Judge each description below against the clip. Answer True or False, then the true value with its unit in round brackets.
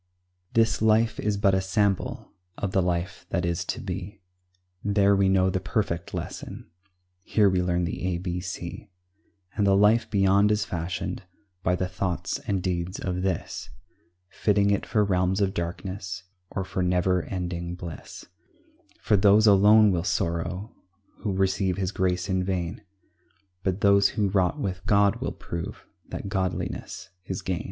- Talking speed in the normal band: True (160 wpm)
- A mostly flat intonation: True (1.9 semitones)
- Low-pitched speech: True (95 Hz)